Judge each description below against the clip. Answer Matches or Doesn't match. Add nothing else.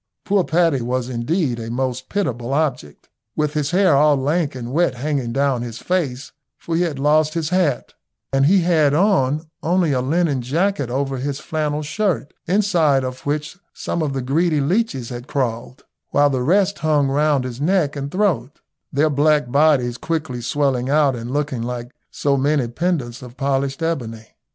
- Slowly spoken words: Doesn't match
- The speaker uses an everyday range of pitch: Matches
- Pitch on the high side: Doesn't match